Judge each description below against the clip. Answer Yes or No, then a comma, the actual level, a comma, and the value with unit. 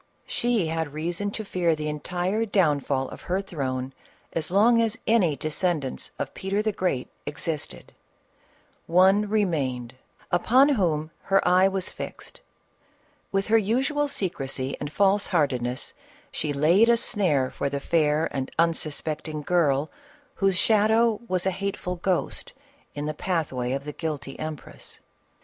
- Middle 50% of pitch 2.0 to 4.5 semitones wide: No, average, 5.1 semitones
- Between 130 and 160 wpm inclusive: Yes, average, 140 wpm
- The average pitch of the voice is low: No, medium, 170 Hz